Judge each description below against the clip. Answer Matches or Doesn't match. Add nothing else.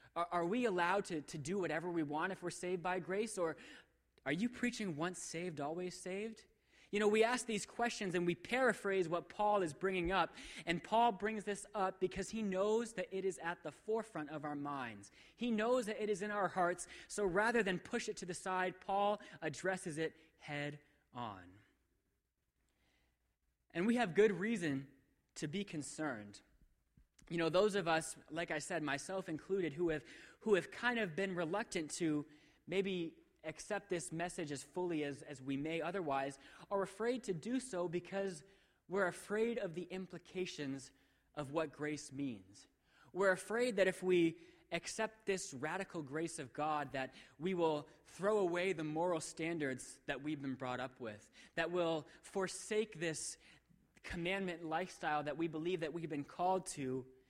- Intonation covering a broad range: Doesn't match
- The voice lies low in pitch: Doesn't match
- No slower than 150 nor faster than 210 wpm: Matches